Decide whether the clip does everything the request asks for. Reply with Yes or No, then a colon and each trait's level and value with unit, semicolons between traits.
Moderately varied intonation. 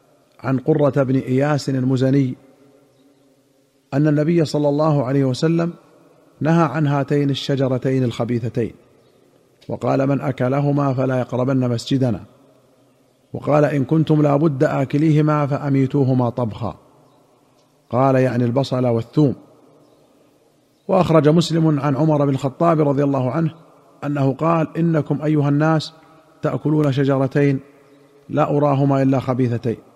No: narrow, 2.3 semitones